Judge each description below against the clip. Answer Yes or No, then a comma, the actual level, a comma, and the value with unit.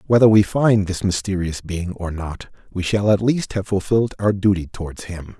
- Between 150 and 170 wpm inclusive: No, average, 200 wpm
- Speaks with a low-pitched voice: Yes, low, 100 Hz